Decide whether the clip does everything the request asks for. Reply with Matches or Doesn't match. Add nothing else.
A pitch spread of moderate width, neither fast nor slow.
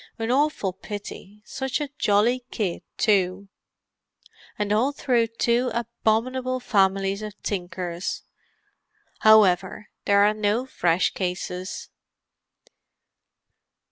Doesn't match